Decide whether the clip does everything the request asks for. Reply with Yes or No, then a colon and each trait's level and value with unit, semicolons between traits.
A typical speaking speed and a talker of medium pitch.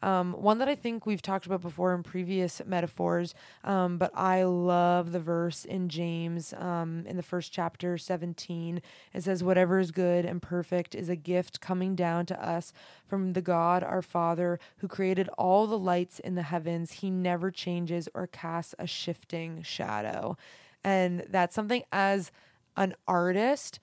Yes: average, 170 wpm; medium, 180 Hz